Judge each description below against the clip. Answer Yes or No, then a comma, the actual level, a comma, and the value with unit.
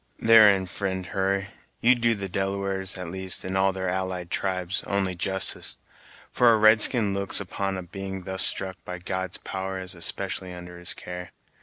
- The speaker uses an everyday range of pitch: No, narrow, 1.2 semitones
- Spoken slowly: No, average, 175 wpm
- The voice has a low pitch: Yes, very low, 95 Hz